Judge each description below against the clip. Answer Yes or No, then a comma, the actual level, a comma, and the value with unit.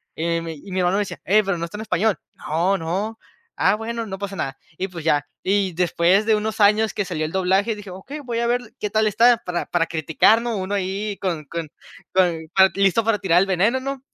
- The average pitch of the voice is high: Yes, high, 195 Hz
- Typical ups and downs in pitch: Yes, average, 3.7 semitones